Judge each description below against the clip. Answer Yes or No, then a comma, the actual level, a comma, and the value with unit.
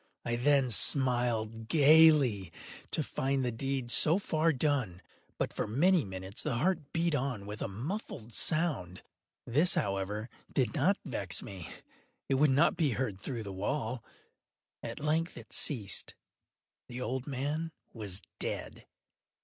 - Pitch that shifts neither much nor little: No, wide, 5.9 semitones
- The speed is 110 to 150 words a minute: Yes, average, 140 wpm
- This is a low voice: Yes, low, 130 Hz